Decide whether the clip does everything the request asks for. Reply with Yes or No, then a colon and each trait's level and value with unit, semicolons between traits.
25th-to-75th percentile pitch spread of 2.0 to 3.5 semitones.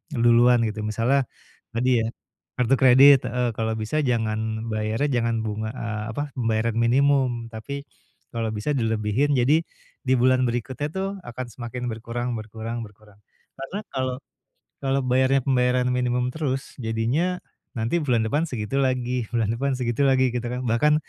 Yes: average, 2.9 semitones